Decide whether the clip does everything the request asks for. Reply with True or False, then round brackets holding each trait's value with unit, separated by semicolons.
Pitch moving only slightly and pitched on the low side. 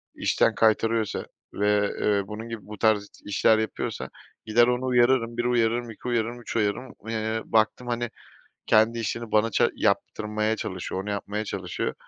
True (1.9 semitones; 110 Hz)